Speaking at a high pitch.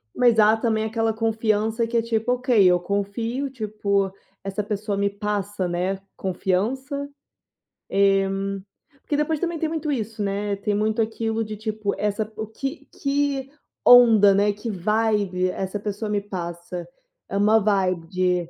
Yes: high, 215 Hz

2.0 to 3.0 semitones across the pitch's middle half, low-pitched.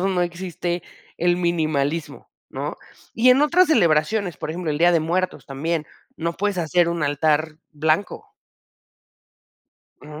No: average, 2.7 semitones; medium, 170 Hz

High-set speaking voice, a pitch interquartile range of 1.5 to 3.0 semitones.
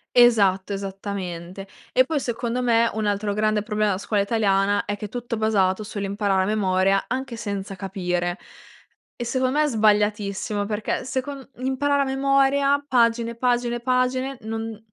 No: high, 215 Hz; average, 3.9 semitones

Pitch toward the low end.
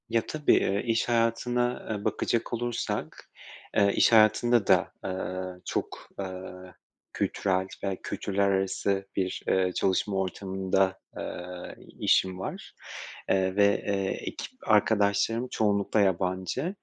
Yes: low, 100 Hz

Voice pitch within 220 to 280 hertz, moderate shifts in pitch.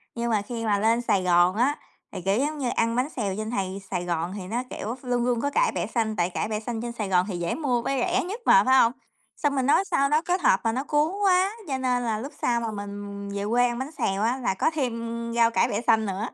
Yes: high, 230 Hz; average, 4.3 semitones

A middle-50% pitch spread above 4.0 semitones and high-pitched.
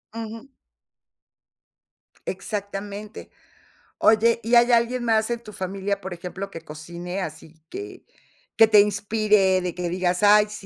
No: average, 3.2 semitones; high, 205 Hz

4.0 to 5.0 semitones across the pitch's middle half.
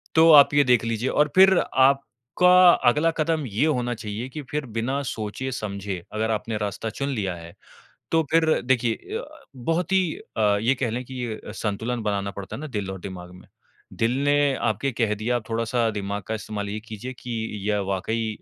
Yes: average, 4.6 semitones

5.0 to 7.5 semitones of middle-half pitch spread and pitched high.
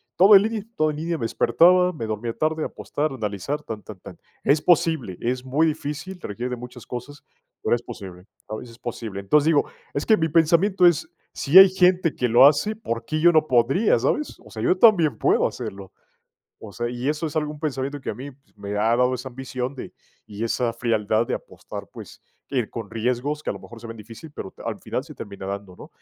No: wide, 5.6 semitones; low, 130 Hz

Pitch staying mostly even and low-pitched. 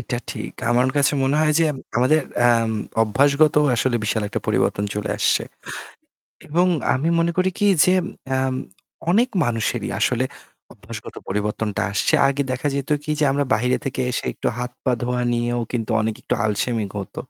No: average, 3.9 semitones; low, 125 Hz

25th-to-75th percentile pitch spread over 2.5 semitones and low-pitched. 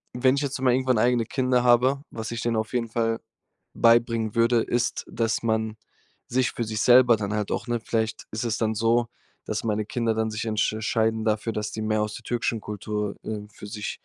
No: narrow, 1.9 semitones; low, 115 Hz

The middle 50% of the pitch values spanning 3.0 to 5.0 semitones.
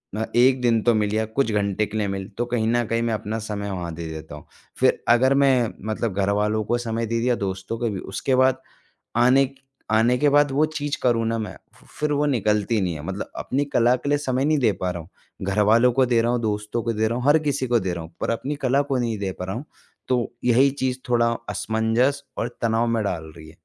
Yes: average, 3.5 semitones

